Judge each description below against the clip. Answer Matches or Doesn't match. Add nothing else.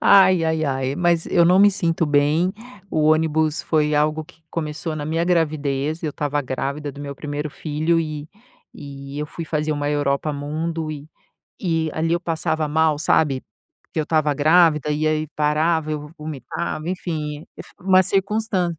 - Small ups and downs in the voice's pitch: Matches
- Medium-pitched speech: Matches